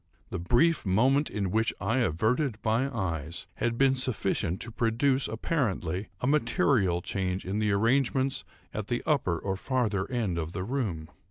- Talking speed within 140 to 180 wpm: Yes, average, 160 wpm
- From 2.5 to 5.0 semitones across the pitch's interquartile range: No, wide, 5.6 semitones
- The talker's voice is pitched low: Yes, low, 110 Hz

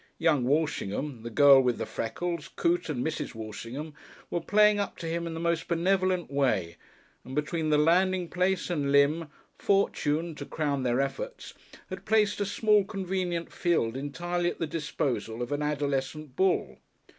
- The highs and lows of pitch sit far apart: No, average, 4.1 semitones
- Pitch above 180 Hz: No, medium, 160 Hz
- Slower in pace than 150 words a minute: No, average, 165 wpm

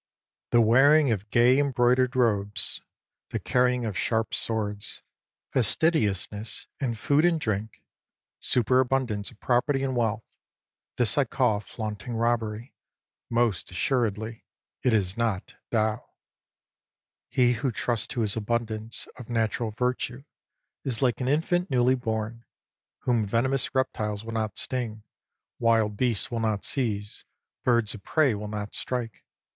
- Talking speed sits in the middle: No, slow, 130 wpm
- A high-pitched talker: No, low, 115 Hz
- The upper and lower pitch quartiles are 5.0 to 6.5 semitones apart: No, average, 2.8 semitones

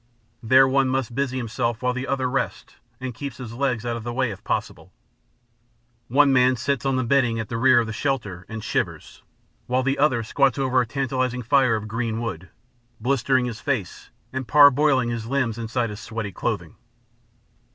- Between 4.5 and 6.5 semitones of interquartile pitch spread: No, average, 2.7 semitones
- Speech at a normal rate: Yes, average, 185 wpm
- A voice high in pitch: No, low, 125 Hz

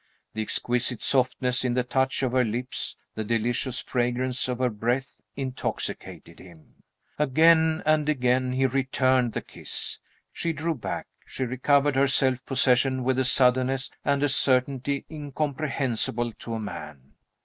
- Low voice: Yes, low, 130 Hz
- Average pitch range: No, narrow, 1.9 semitones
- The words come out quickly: No, average, 145 wpm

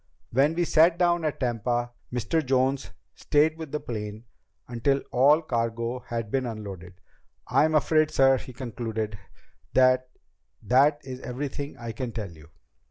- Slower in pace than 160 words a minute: Yes, average, 145 wpm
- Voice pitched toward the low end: Yes, low, 130 Hz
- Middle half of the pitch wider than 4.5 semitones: No, average, 4.1 semitones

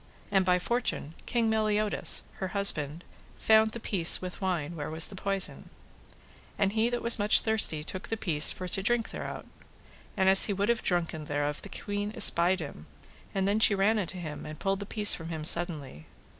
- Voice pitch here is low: No, high, 190 Hz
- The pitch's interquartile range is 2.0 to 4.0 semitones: No, average, 4.4 semitones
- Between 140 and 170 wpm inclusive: No, average, 195 wpm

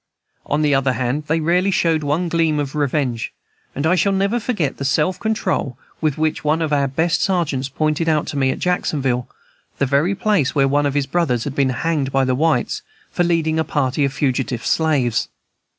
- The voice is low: No, medium, 150 Hz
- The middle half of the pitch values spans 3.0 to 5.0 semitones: Yes, average, 3.4 semitones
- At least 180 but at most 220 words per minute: Yes, average, 200 wpm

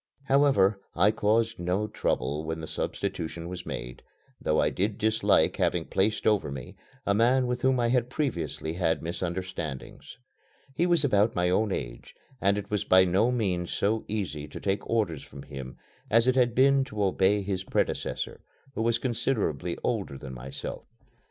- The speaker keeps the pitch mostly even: No, average, 5.3 semitones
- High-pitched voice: No, low, 100 Hz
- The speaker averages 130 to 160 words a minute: No, average, 170 wpm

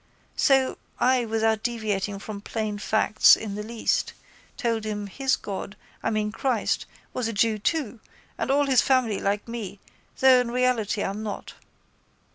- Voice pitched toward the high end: Yes, high, 220 Hz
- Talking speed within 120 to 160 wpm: Yes, average, 155 wpm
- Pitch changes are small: No, average, 3.2 semitones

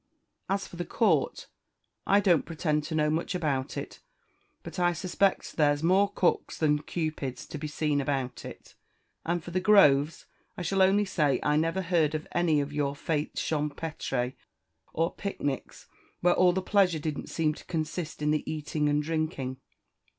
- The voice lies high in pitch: No, medium, 155 Hz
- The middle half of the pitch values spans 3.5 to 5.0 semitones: No, average, 3.1 semitones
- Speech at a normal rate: Yes, average, 170 wpm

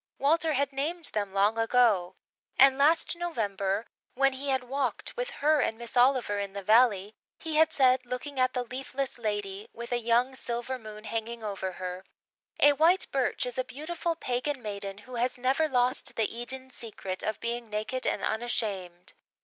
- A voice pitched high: Yes, high, 245 Hz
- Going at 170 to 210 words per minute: Yes, average, 175 wpm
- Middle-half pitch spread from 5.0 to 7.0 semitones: No, average, 4.3 semitones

